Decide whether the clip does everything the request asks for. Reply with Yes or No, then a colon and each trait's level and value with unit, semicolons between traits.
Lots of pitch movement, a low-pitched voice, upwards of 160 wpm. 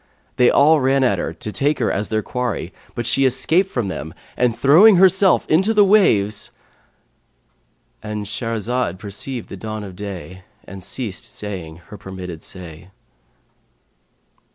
No: wide, 6.0 semitones; low, 110 Hz; average, 140 wpm